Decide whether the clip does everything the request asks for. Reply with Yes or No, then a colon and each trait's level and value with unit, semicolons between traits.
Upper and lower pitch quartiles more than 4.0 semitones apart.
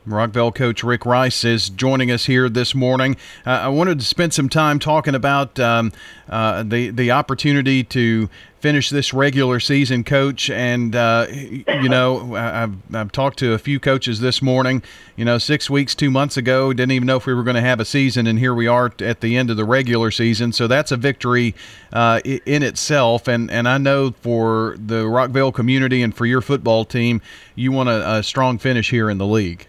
No: narrow, 2.6 semitones